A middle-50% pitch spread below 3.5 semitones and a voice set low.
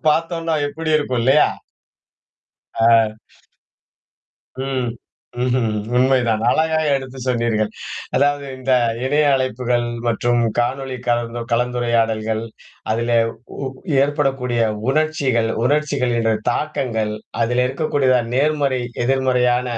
Yes: average, 2.9 semitones; low, 125 Hz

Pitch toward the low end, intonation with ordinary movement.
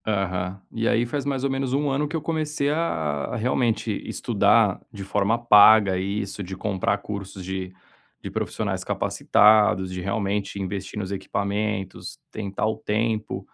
Yes: low, 105 Hz; average, 3.4 semitones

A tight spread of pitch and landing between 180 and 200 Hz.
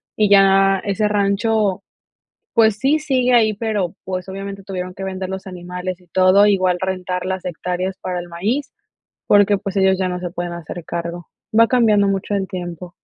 Yes: narrow, 2.1 semitones; high, 190 Hz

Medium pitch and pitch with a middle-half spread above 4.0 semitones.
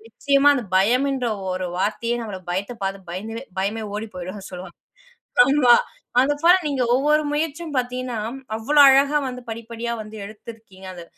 No: high, 235 Hz; wide, 5.4 semitones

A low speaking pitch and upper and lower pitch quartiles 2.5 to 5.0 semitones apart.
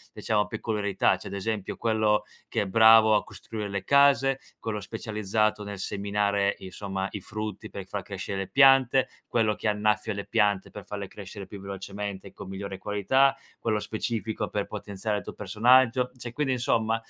No: low, 105 Hz; narrow, 2.1 semitones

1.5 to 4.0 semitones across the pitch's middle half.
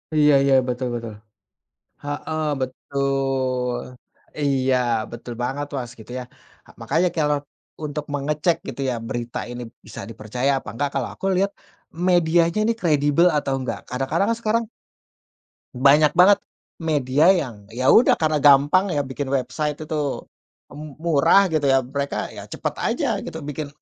Yes: average, 3.5 semitones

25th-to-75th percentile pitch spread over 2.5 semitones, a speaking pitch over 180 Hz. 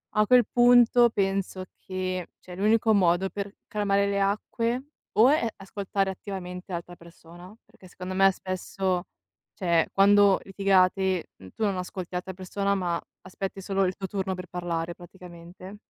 No: narrow, 1.8 semitones; high, 190 Hz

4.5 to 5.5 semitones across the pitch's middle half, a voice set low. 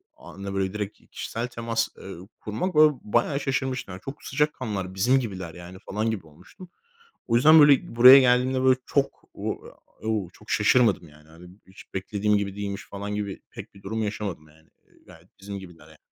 Yes: average, 4.8 semitones; low, 105 Hz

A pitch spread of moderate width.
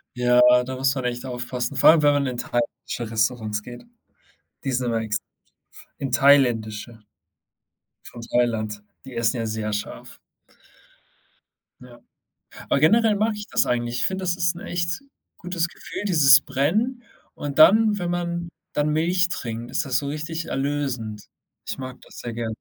No: wide, 5.9 semitones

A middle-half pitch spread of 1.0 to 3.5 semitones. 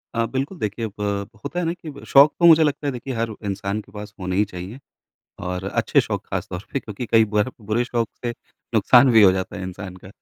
No: average, 5.1 semitones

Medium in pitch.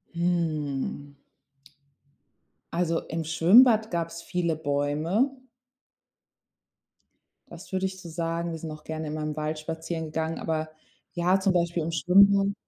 Yes: medium, 165 Hz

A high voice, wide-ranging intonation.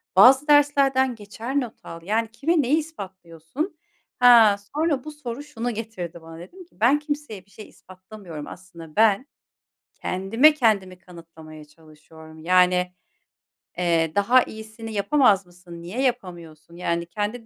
Yes: high, 205 Hz; wide, 6.8 semitones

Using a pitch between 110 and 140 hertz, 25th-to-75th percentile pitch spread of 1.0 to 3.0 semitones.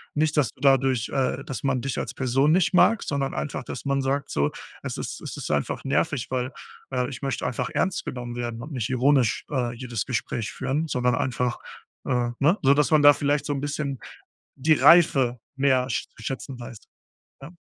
Yes: low, 135 Hz; narrow, 2.4 semitones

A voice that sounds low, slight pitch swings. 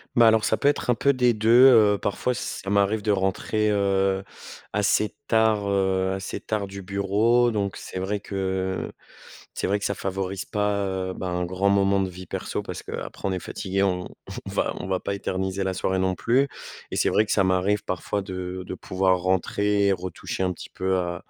Yes: very low, 95 Hz; narrow, 1.8 semitones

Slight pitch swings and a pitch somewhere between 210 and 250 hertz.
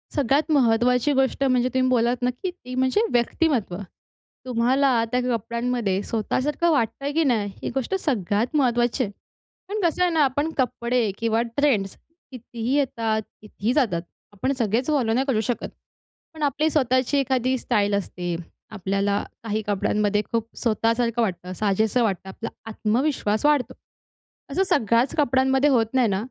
No: average, 3.6 semitones; high, 245 Hz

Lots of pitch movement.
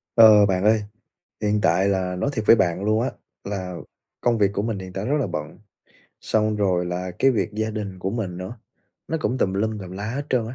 No: average, 2.9 semitones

